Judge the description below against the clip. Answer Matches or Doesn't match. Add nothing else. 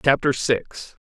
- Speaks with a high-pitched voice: Doesn't match